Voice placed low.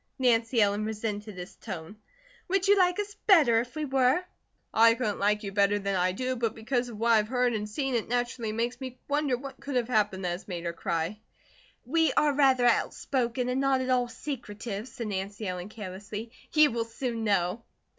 No: high, 230 Hz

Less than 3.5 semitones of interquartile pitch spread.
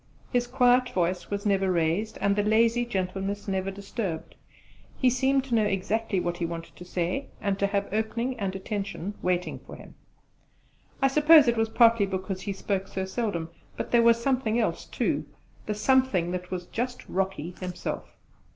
No: average, 3.9 semitones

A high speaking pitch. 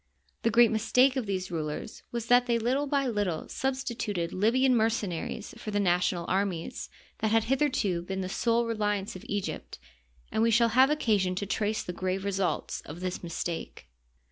Yes: high, 210 Hz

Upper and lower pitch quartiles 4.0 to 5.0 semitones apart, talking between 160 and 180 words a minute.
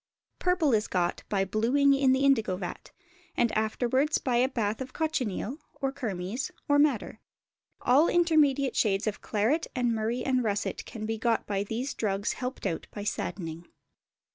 Yes: average, 4.7 semitones; average, 165 wpm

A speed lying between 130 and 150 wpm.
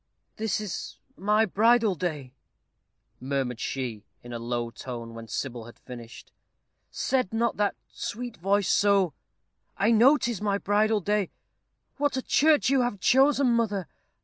Yes: average, 145 wpm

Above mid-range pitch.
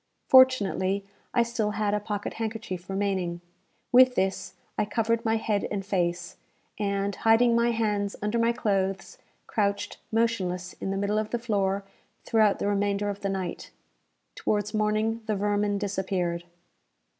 Yes: high, 205 Hz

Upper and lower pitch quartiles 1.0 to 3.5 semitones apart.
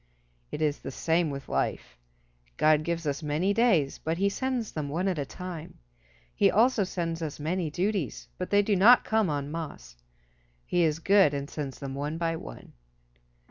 No: average, 4.6 semitones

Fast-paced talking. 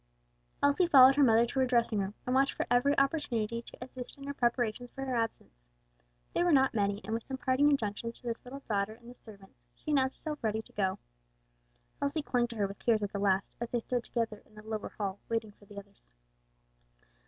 Yes: fast, 220 wpm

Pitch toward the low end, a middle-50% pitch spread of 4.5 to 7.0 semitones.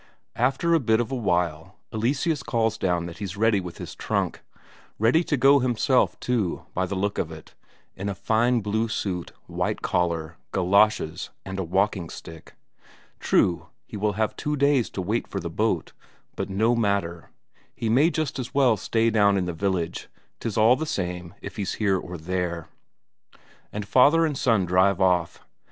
Yes: low, 100 Hz; average, 4.9 semitones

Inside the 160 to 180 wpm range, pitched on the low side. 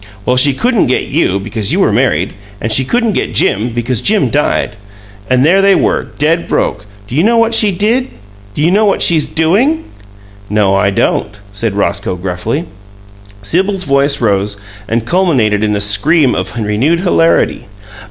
Yes: average, 170 wpm; low, 130 Hz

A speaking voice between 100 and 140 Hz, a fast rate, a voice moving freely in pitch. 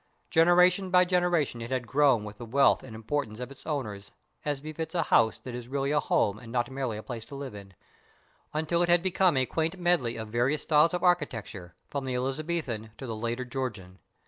Yes: low, 135 Hz; fast, 210 wpm; wide, 5.7 semitones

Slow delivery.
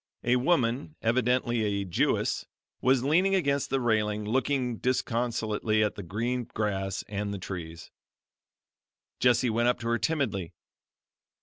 Yes: slow, 130 wpm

